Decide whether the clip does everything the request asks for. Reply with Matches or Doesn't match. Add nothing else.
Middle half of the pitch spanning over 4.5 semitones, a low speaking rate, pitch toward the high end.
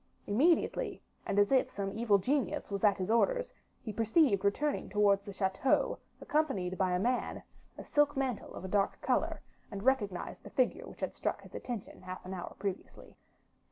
Doesn't match